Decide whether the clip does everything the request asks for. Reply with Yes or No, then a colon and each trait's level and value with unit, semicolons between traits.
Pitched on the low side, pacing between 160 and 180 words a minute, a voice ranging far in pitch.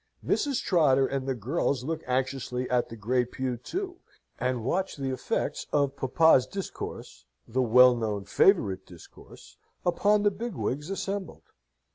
No: low, 130 Hz; average, 145 wpm; wide, 6.0 semitones